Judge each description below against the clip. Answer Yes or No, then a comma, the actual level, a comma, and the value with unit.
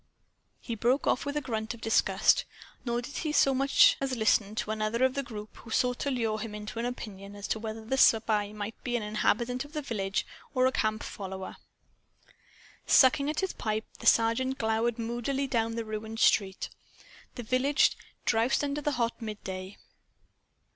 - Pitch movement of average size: Yes, average, 3.2 semitones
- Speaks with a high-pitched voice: Yes, high, 230 Hz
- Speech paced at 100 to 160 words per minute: No, average, 180 wpm